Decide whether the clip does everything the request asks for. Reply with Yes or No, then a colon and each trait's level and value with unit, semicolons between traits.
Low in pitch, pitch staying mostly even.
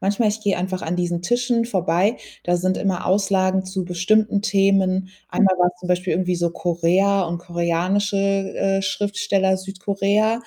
No: high, 190 Hz; narrow, 1.9 semitones